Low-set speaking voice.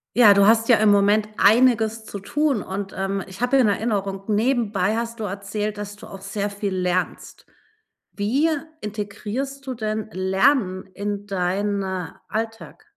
No: high, 205 Hz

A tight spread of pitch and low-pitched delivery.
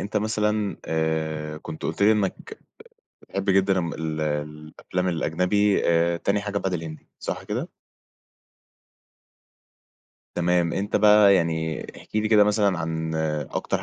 No: average, 4.1 semitones; very low, 90 Hz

